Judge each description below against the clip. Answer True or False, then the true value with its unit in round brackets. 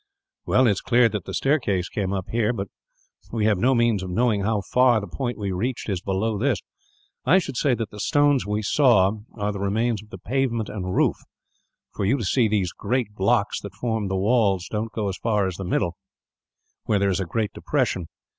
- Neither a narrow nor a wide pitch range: True (3.5 semitones)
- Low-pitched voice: True (105 Hz)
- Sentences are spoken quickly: True (210 wpm)